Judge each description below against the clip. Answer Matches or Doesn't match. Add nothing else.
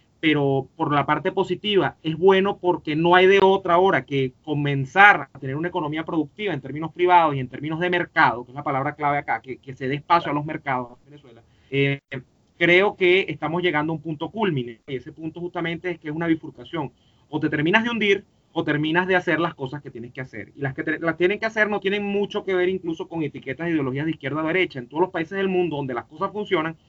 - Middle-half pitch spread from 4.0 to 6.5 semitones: Matches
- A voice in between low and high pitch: Matches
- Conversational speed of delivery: Doesn't match